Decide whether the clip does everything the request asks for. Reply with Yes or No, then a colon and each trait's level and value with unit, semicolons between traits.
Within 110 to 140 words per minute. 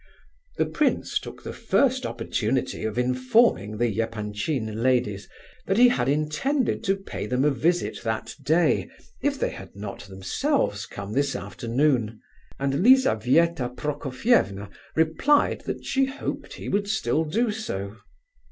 Yes: slow, 135 wpm